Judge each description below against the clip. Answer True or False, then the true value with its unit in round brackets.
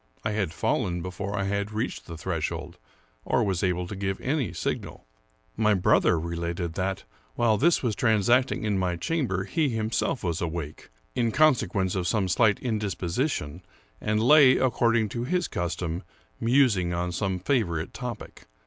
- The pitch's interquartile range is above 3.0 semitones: True (4.9 semitones)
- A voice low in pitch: True (100 Hz)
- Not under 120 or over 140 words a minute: False (160 wpm)